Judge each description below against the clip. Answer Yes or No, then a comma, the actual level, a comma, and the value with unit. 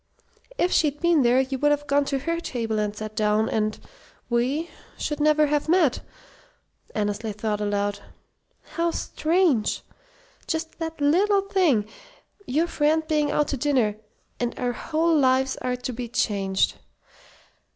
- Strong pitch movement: Yes, wide, 6.2 semitones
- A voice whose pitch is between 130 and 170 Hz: No, very high, 275 Hz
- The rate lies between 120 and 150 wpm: Yes, average, 145 wpm